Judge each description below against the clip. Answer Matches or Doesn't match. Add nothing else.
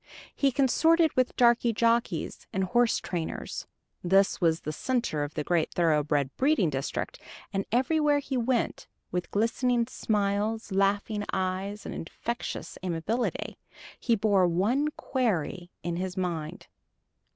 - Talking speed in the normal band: Doesn't match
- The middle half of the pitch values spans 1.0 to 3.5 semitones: Doesn't match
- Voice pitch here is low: Doesn't match